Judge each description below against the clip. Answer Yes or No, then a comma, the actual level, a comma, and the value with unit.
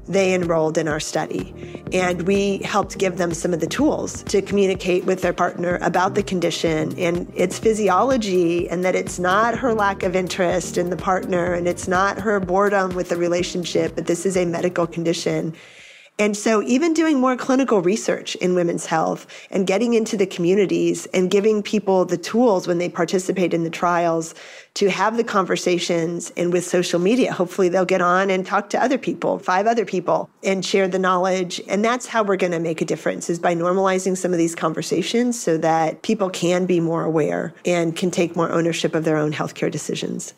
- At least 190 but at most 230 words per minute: Yes, average, 200 wpm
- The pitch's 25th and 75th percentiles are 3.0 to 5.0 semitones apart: No, narrow, 2.4 semitones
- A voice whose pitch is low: No, medium, 180 Hz